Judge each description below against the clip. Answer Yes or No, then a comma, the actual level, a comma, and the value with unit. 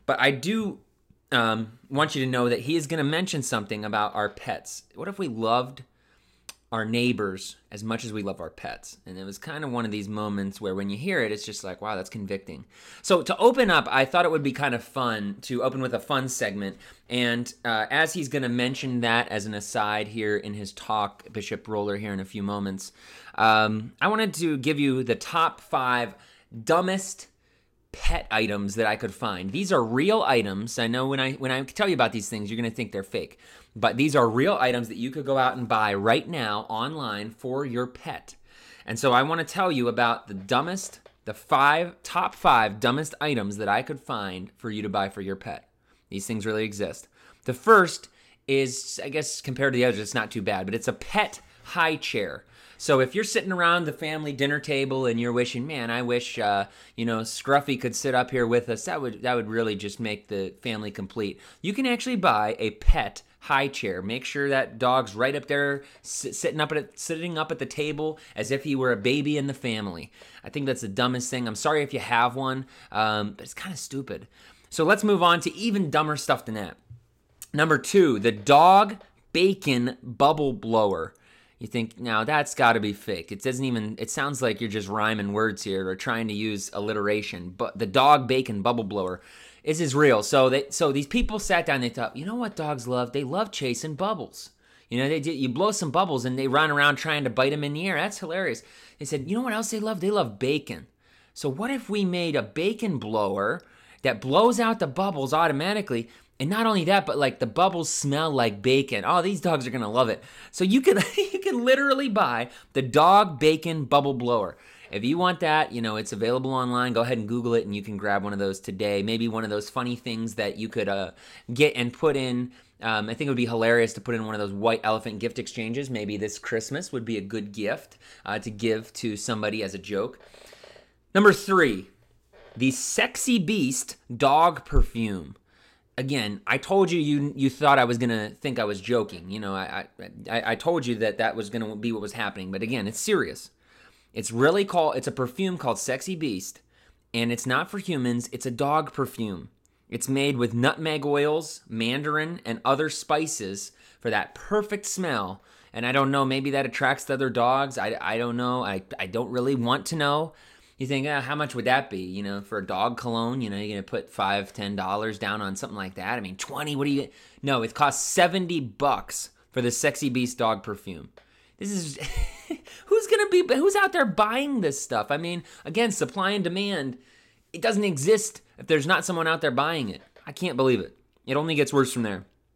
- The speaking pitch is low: Yes, low, 125 Hz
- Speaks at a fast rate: Yes, fast, 220 wpm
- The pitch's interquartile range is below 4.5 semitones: No, wide, 5.5 semitones